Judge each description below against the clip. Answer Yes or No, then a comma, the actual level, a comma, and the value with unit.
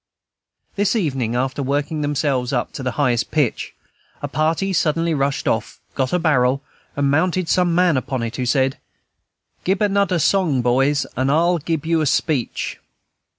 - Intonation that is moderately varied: Yes, average, 4.3 semitones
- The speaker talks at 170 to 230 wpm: No, average, 160 wpm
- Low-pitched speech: No, medium, 145 Hz